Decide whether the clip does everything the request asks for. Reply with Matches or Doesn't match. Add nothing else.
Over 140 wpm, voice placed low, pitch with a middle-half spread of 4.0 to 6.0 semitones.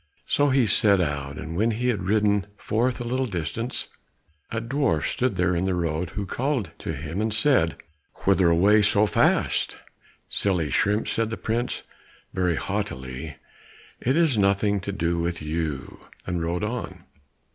Matches